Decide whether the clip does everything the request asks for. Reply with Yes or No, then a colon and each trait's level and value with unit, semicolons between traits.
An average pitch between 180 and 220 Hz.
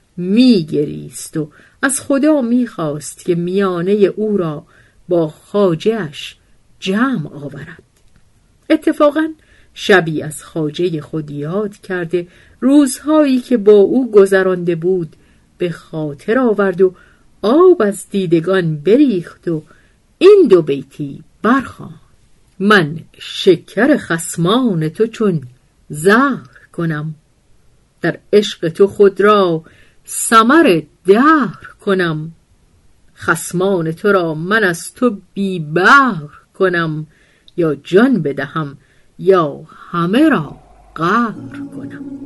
Yes: medium, 185 Hz